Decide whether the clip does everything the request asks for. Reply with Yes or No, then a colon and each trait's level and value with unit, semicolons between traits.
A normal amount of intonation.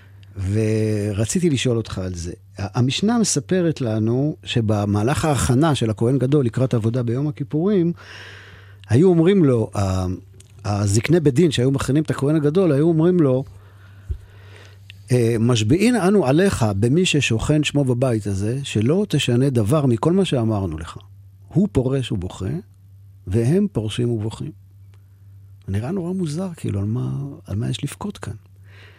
No: wide, 6.7 semitones